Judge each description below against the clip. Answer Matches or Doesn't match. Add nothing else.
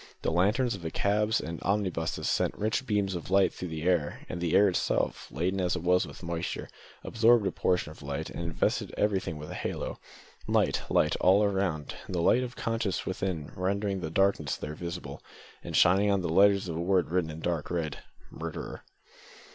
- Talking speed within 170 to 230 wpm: Matches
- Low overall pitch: Matches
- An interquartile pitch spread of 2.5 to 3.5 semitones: Matches